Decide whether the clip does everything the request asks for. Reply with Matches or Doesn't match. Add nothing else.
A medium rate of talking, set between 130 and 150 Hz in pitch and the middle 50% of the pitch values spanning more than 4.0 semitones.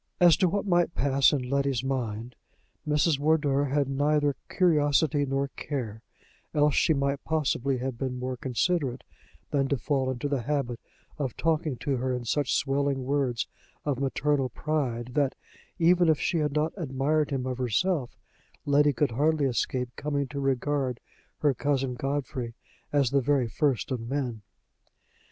Doesn't match